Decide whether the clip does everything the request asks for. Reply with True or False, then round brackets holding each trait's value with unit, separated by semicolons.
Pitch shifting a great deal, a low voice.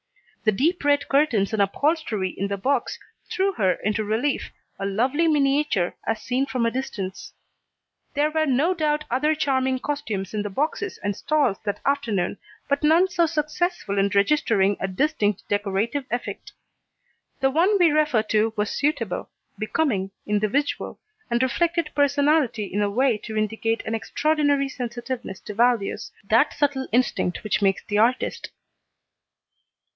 False (6.2 semitones; 255 Hz)